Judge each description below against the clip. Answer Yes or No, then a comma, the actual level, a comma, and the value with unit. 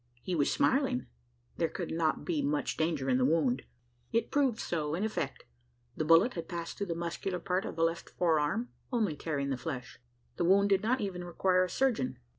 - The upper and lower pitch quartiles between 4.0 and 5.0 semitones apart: Yes, average, 4.5 semitones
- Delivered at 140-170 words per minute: No, average, 200 wpm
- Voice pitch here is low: No, medium, 170 Hz